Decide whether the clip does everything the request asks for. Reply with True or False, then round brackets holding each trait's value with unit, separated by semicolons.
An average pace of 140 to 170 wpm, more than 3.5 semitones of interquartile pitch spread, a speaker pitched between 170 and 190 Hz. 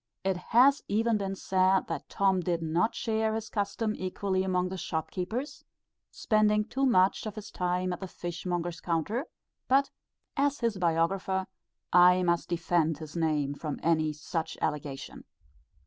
True (155 wpm; 4.0 semitones; 185 Hz)